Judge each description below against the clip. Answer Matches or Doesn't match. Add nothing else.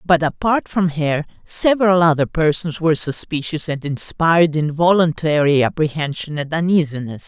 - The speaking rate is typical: Doesn't match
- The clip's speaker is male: Doesn't match